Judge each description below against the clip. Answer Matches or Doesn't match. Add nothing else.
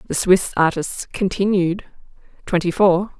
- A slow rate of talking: Matches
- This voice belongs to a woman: Matches